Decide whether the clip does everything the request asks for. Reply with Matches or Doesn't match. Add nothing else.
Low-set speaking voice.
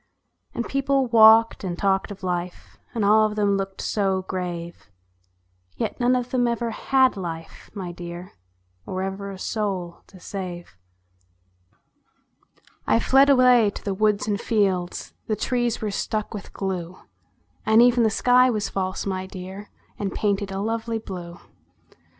Doesn't match